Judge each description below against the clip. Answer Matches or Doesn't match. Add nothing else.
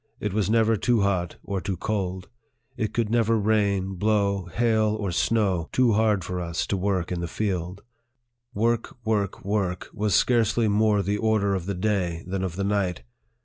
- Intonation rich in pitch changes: Doesn't match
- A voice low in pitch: Matches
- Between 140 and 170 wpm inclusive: Doesn't match